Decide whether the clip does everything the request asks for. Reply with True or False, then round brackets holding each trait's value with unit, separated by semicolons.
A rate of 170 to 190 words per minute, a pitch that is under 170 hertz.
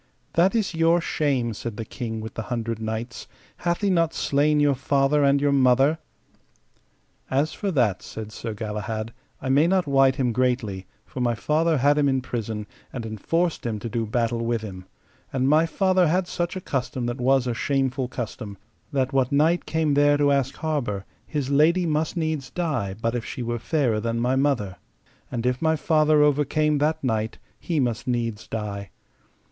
True (185 wpm; 135 Hz)